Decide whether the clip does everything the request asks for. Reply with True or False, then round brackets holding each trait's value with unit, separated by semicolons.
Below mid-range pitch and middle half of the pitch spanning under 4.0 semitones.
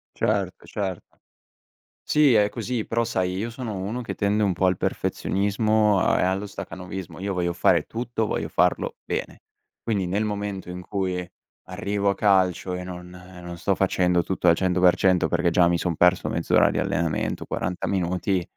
True (95 Hz; 2.4 semitones)